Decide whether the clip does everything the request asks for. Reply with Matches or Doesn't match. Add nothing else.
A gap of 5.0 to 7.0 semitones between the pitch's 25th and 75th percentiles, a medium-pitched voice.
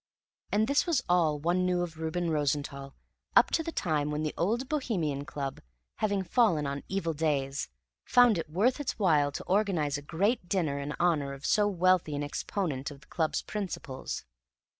Matches